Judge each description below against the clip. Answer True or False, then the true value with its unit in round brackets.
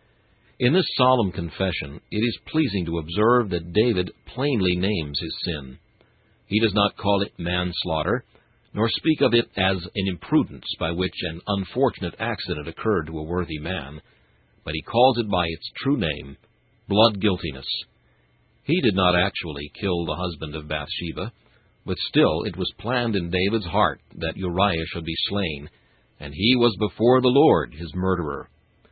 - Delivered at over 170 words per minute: False (160 wpm)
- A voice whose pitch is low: True (95 Hz)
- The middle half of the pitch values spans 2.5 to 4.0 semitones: False (4.9 semitones)